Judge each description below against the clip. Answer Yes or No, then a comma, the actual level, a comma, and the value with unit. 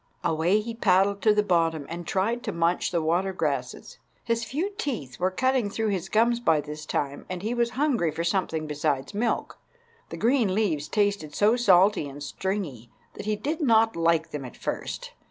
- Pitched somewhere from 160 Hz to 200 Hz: Yes, high, 190 Hz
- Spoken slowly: No, average, 190 wpm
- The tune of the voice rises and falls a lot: Yes, wide, 5.9 semitones